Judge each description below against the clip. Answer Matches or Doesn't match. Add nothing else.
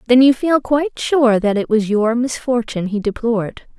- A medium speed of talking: Matches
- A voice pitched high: Matches